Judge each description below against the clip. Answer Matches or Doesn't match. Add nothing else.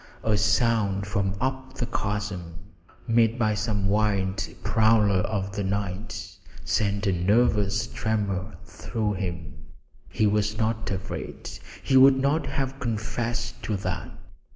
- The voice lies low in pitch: Matches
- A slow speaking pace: Matches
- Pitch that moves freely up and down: Doesn't match